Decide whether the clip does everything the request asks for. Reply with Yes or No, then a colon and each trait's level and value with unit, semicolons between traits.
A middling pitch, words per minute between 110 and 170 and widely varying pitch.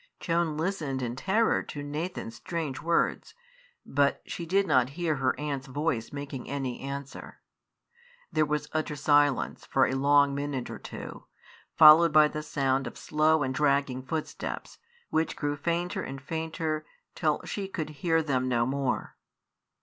No: medium, 145 Hz; average, 150 wpm; average, 2.9 semitones